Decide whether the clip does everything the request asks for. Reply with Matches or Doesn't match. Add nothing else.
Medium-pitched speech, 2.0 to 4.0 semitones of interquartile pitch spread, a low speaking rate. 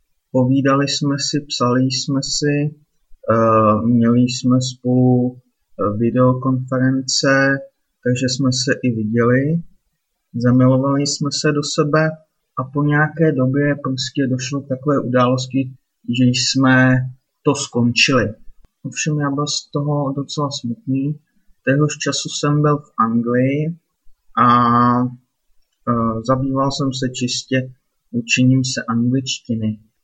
Doesn't match